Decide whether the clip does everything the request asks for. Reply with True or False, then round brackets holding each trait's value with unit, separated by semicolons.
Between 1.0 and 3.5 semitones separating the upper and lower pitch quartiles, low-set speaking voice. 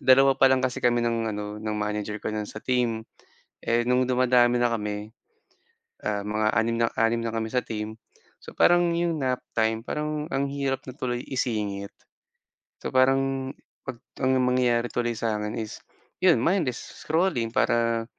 True (2.8 semitones; 120 Hz)